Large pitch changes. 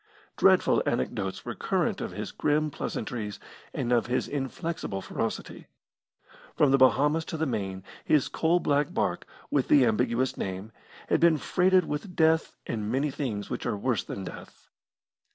Yes: wide, 6.3 semitones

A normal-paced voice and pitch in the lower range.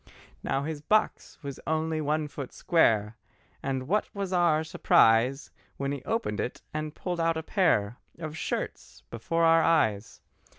No: average, 155 wpm; medium, 155 Hz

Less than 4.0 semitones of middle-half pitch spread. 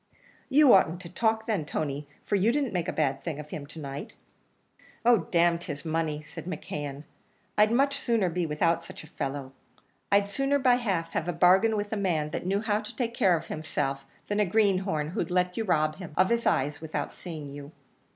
No: wide, 5.5 semitones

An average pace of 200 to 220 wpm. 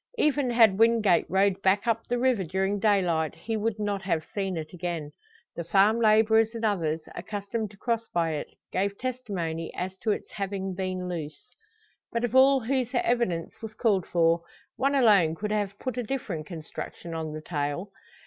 No: average, 175 wpm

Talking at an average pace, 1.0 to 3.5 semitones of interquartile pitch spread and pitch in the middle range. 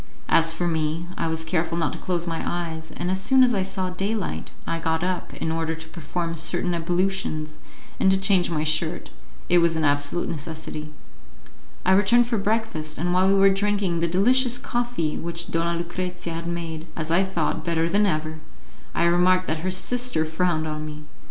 Yes: average, 190 wpm; average, 2.8 semitones; medium, 170 Hz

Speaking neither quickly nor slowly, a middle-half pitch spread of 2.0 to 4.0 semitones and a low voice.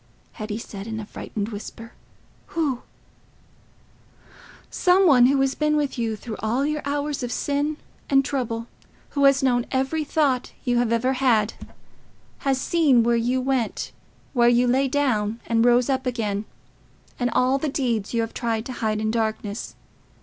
No: average, 155 wpm; average, 3.3 semitones; high, 245 Hz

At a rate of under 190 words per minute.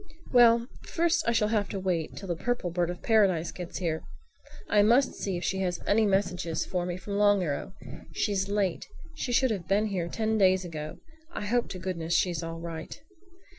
No: average, 200 wpm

